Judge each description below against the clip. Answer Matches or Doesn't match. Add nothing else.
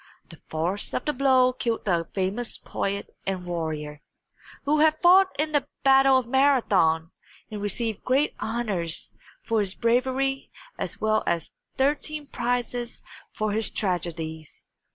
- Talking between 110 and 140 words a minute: Matches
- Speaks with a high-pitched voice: Matches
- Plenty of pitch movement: Matches